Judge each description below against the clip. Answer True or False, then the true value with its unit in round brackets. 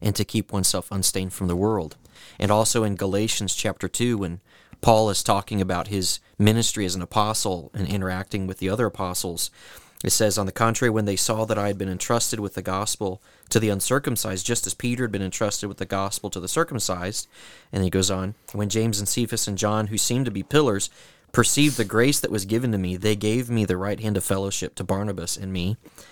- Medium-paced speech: False (220 wpm)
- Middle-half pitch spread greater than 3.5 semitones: False (2.8 semitones)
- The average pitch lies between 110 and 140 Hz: False (100 Hz)